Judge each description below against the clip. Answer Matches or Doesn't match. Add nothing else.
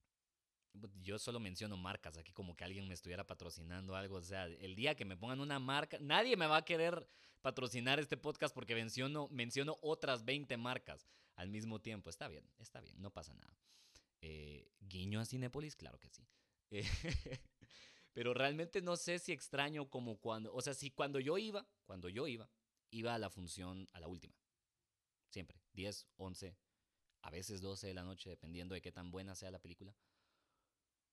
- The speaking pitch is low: Matches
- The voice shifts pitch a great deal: Matches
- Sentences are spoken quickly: Doesn't match